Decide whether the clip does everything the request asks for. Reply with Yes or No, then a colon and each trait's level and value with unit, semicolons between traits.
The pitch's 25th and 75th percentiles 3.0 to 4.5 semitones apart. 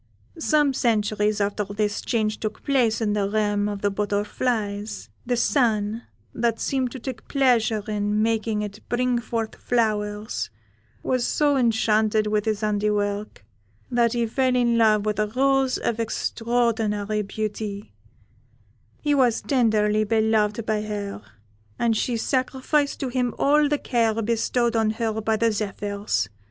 No: narrow, 2.4 semitones